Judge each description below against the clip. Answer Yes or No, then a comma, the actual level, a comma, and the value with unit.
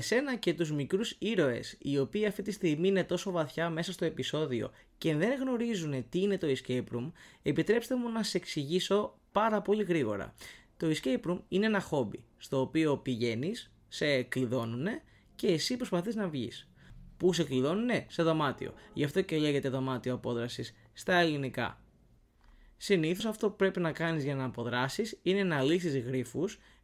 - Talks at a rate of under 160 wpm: No, average, 165 wpm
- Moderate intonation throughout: No, wide, 6.9 semitones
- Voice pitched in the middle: Yes, medium, 165 Hz